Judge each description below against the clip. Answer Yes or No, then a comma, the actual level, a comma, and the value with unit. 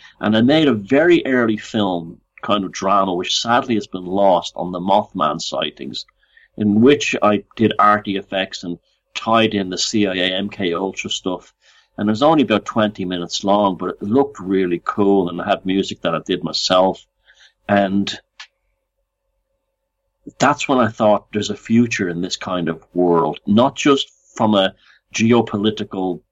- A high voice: No, low, 105 Hz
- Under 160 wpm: No, average, 165 wpm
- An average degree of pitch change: Yes, average, 3.2 semitones